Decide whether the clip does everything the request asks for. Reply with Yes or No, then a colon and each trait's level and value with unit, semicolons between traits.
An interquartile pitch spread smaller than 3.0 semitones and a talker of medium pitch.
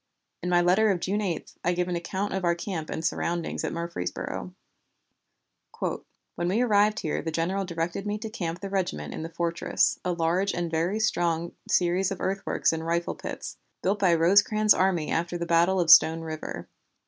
Yes: narrow, 2.6 semitones; medium, 175 Hz